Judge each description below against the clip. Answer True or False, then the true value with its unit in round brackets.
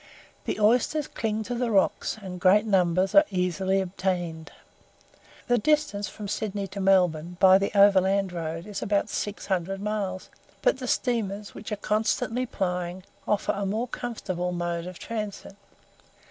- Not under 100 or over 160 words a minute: True (150 wpm)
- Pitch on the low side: False (195 Hz)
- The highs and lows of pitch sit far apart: False (2.7 semitones)